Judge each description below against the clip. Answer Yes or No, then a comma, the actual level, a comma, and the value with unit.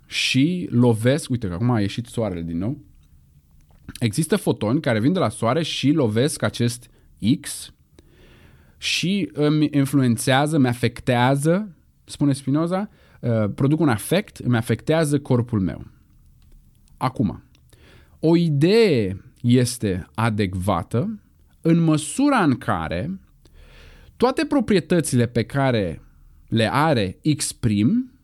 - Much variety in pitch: Yes, wide, 7.0 semitones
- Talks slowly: Yes, slow, 110 wpm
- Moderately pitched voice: No, low, 120 Hz